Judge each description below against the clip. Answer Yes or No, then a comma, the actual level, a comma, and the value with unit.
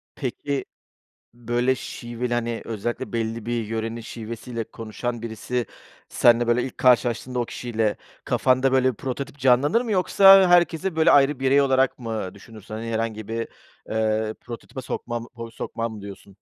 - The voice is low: Yes, low, 120 Hz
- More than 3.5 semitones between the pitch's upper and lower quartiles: No, narrow, 2.5 semitones